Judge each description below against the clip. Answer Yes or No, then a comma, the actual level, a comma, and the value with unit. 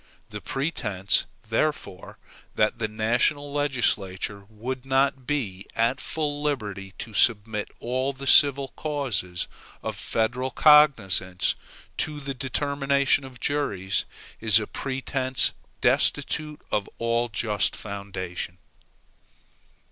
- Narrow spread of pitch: No, average, 5.1 semitones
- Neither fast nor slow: No, slow, 105 wpm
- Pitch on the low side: Yes, low, 125 Hz